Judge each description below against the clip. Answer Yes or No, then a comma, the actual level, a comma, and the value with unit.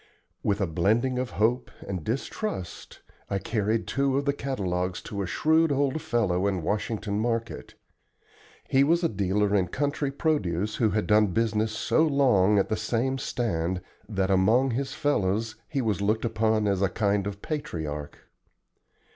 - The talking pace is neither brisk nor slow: Yes, average, 160 wpm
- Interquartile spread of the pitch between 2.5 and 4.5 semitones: No, average, 5.2 semitones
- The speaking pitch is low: Yes, low, 110 Hz